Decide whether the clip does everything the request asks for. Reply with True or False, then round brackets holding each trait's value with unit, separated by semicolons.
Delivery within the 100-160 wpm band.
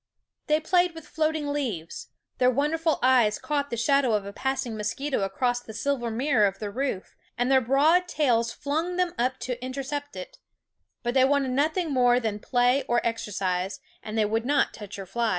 False (185 wpm)